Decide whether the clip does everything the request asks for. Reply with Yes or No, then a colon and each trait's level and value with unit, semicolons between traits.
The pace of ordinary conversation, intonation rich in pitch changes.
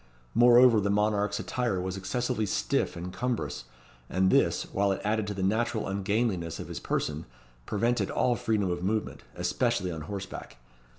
No: average, 160 wpm; average, 3.8 semitones